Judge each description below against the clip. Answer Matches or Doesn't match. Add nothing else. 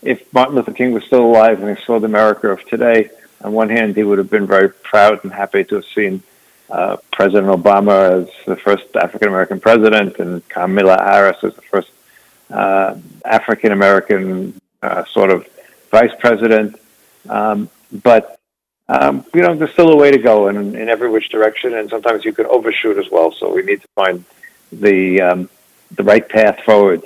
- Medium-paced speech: Matches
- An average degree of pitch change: Matches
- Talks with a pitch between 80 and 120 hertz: Matches